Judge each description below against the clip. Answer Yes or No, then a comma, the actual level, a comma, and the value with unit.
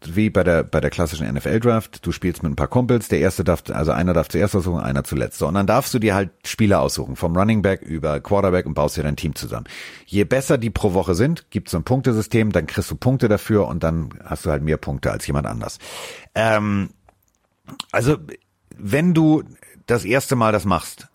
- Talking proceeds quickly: Yes, fast, 215 wpm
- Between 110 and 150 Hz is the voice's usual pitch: No, low, 100 Hz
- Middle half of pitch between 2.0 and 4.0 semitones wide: No, wide, 5.6 semitones